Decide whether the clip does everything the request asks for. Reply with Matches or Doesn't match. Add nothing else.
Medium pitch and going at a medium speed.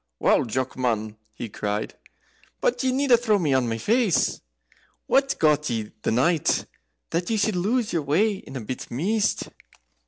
Matches